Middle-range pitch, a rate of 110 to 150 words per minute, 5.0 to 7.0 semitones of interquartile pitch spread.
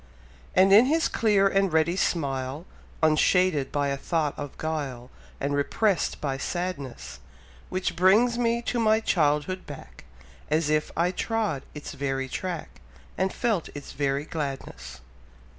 Yes: medium, 160 Hz; average, 140 wpm; wide, 5.5 semitones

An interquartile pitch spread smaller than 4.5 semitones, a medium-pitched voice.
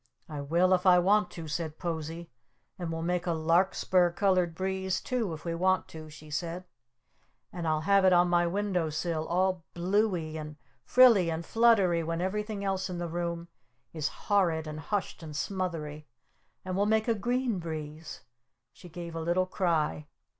Yes: average, 2.8 semitones; medium, 175 Hz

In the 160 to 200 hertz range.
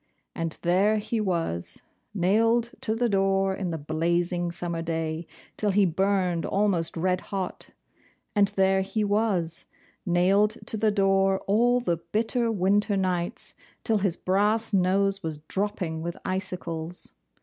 Yes: high, 190 Hz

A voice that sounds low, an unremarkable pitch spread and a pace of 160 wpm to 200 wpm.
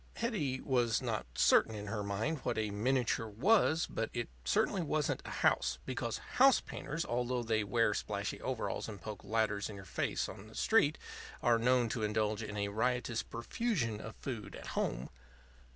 Yes: low, 115 Hz; average, 3.7 semitones; average, 175 wpm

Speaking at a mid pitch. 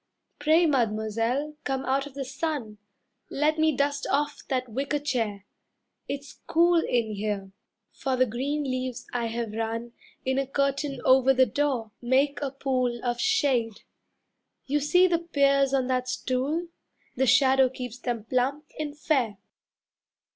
No: very high, 265 Hz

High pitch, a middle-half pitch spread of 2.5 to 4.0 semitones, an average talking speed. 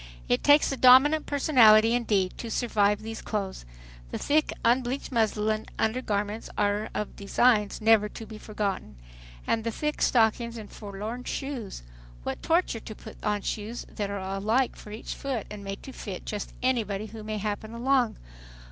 Yes: high, 220 Hz; average, 2.8 semitones; average, 165 wpm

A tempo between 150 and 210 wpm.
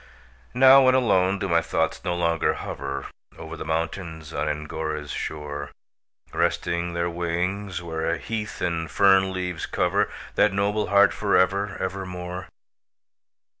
No: slow, 135 wpm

